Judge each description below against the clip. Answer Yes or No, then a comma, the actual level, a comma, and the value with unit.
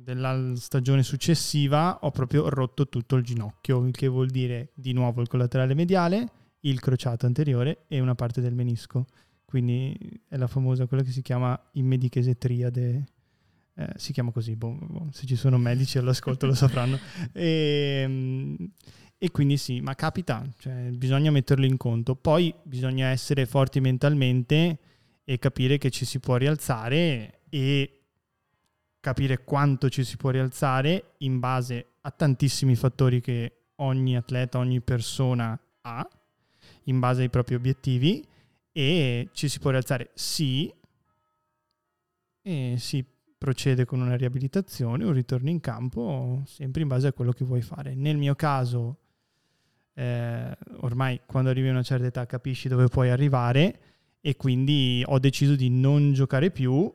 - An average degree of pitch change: No, narrow, 2.0 semitones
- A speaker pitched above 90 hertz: Yes, low, 130 Hz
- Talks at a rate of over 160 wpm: No, average, 150 wpm